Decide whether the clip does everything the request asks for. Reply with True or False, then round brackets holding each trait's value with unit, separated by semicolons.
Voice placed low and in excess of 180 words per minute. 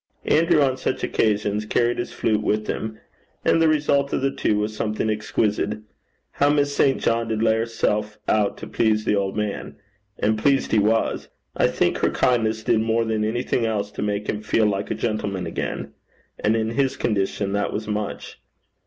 True (110 Hz; 190 wpm)